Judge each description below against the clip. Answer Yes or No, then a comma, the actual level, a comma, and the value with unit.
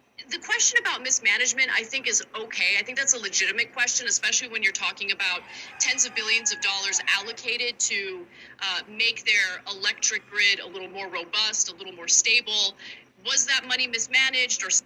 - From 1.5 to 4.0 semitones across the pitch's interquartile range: No, average, 4.8 semitones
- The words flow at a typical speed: Yes, average, 180 wpm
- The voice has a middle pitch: No, high, 230 Hz